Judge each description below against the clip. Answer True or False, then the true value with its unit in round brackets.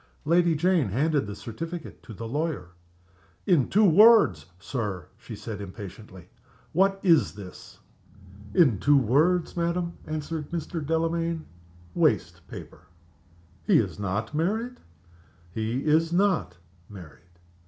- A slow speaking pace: True (120 wpm)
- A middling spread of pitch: False (8.6 semitones)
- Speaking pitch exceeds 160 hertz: False (150 Hz)